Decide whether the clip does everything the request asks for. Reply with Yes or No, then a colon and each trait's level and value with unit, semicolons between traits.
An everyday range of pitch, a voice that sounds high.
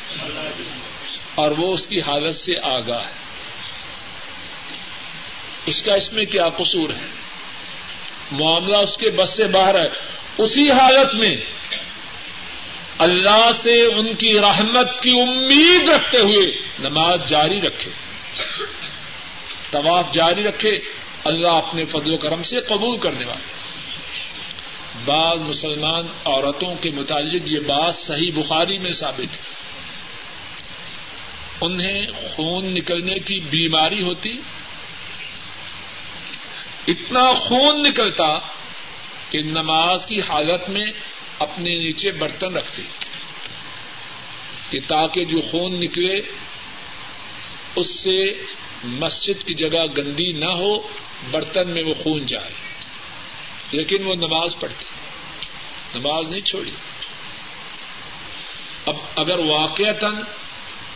No: average, 5.0 semitones; medium, 175 Hz